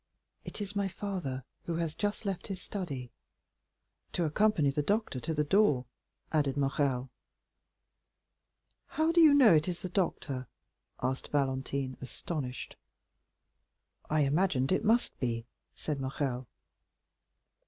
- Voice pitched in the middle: Yes, medium, 150 Hz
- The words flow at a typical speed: No, slow, 125 wpm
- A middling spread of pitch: No, wide, 6.6 semitones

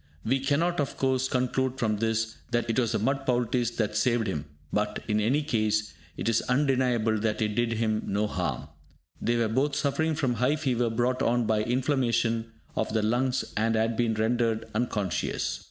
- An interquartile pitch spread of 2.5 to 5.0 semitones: Yes, average, 2.9 semitones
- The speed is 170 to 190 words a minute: Yes, average, 185 wpm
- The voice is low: Yes, low, 115 Hz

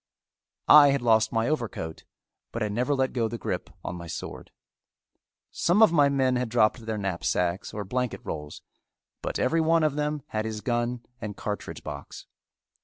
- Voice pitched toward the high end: No, low, 120 Hz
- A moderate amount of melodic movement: Yes, average, 4.7 semitones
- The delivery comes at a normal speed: Yes, average, 175 wpm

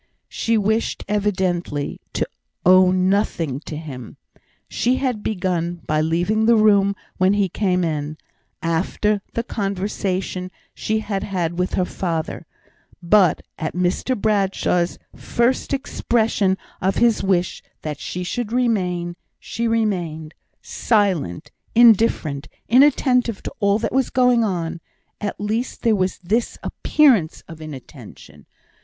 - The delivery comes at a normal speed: No, slow, 125 wpm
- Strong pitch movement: No, average, 4.1 semitones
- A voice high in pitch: Yes, high, 195 Hz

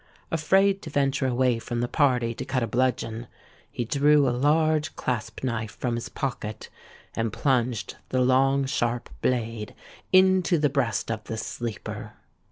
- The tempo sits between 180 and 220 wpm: No, average, 155 wpm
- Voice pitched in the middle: No, low, 125 Hz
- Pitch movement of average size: Yes, average, 3.5 semitones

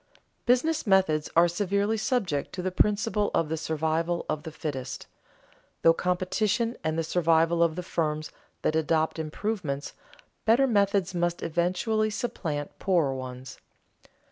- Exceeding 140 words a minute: No, slow, 135 wpm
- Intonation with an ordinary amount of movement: Yes, average, 4.4 semitones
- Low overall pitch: No, medium, 170 Hz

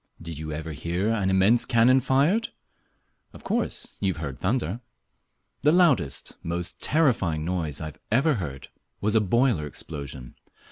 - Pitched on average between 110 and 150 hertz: No, very low, 95 Hz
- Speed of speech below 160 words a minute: Yes, average, 145 wpm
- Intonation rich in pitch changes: Yes, wide, 8.0 semitones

